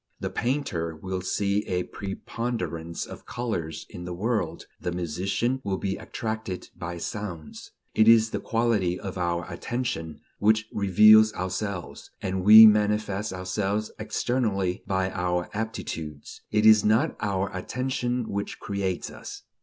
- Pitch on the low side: Yes, low, 100 Hz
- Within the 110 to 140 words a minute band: Yes, slow, 135 wpm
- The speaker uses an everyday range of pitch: Yes, average, 3.3 semitones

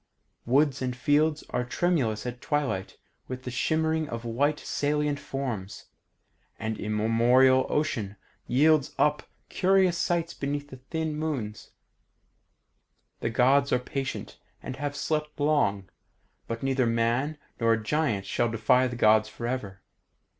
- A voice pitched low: Yes, low, 130 Hz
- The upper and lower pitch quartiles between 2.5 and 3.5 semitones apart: No, average, 4.5 semitones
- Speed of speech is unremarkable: No, slow, 125 wpm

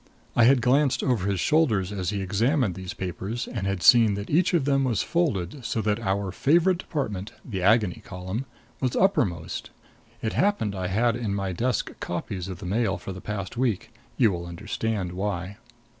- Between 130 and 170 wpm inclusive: No, average, 185 wpm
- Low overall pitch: Yes, low, 105 Hz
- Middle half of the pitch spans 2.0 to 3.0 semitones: No, average, 4.8 semitones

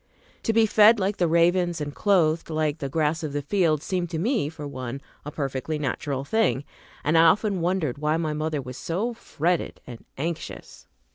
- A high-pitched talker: No, medium, 160 Hz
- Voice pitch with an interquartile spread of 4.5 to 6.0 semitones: No, average, 3.8 semitones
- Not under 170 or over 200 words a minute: Yes, average, 190 wpm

